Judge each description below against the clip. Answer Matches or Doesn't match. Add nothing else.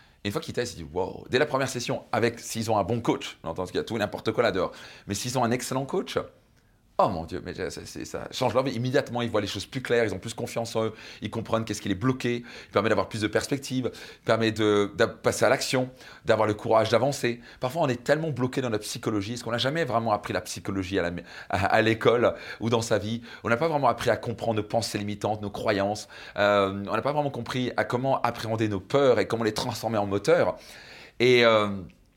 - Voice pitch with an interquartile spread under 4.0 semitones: Matches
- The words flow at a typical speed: Doesn't match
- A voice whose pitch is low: Matches